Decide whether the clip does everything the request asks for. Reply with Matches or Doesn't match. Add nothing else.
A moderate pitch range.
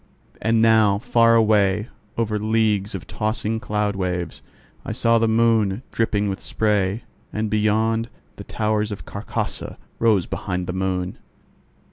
Doesn't match